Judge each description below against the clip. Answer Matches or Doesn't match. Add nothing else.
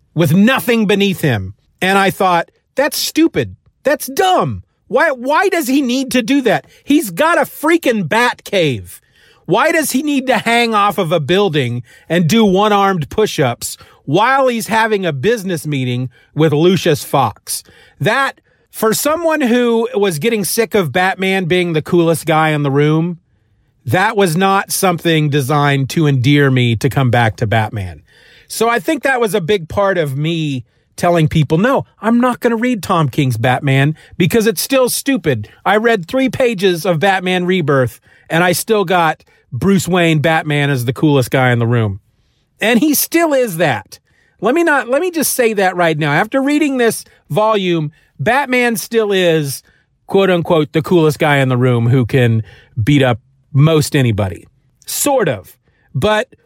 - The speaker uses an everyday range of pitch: Doesn't match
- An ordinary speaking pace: Matches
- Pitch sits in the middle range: Matches